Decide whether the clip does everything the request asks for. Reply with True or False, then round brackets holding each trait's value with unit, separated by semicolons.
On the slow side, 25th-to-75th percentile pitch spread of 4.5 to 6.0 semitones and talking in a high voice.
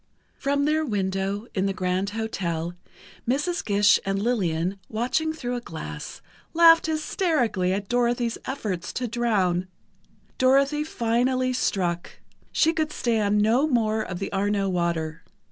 True (130 wpm; 5.2 semitones; 220 Hz)